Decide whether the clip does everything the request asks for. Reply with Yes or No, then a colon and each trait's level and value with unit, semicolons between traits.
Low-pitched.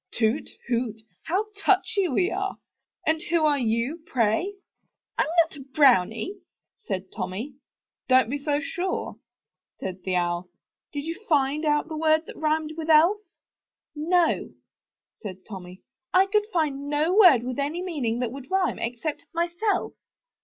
No: very high, 295 Hz